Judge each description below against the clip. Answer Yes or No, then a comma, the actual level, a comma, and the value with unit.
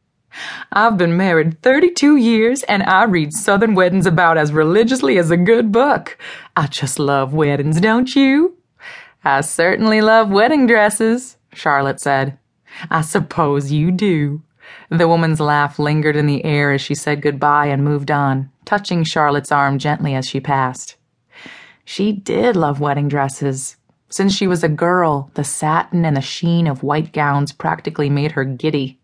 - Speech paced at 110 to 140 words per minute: No, average, 165 wpm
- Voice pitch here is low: No, medium, 155 Hz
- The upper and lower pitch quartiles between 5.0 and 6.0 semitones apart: Yes, wide, 5.6 semitones